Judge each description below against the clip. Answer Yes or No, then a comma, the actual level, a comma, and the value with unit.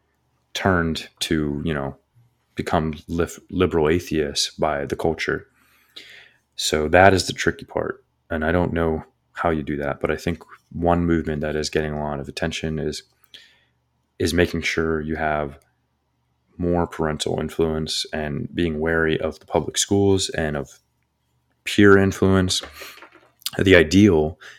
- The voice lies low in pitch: Yes, very low, 80 Hz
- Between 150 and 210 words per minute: No, average, 140 wpm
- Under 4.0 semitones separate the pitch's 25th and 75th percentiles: Yes, narrow, 2.5 semitones